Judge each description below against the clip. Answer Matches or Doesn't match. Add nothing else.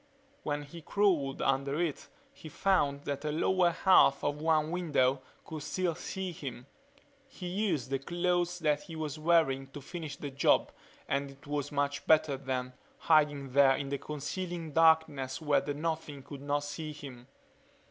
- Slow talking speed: Doesn't match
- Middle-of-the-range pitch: Matches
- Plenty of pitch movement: Doesn't match